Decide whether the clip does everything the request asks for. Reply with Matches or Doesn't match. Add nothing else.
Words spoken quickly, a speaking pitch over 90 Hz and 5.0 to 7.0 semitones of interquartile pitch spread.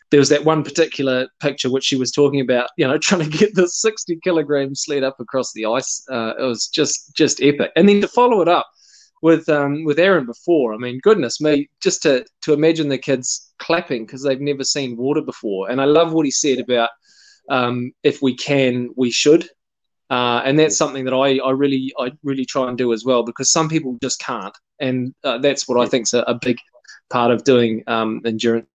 Doesn't match